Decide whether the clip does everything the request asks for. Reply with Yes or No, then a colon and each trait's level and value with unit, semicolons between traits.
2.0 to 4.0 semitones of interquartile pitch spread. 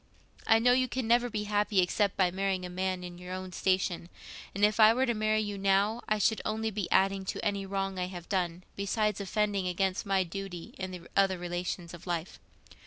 Yes: narrow, 2.6 semitones